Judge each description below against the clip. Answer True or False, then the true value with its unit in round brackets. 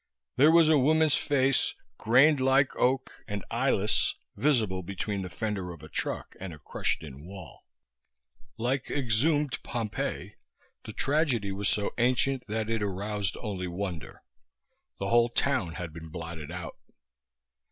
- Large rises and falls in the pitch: True (6.2 semitones)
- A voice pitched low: True (110 Hz)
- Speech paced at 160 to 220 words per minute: False (140 wpm)